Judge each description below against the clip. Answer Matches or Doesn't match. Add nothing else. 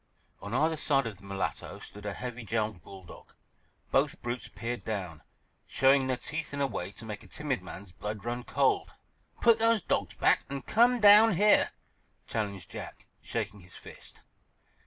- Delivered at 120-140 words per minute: Doesn't match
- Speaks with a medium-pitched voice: Doesn't match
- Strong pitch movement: Matches